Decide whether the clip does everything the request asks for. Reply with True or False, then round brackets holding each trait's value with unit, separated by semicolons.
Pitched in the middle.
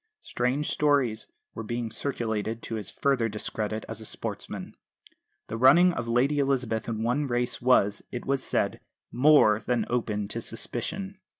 False (120 Hz)